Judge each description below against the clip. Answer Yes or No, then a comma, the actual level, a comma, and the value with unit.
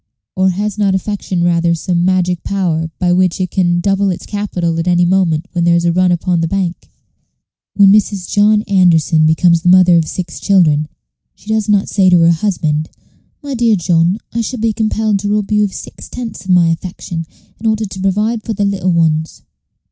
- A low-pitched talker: No, medium, 185 Hz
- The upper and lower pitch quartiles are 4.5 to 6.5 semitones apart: No, average, 3.1 semitones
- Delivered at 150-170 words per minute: No, average, 200 wpm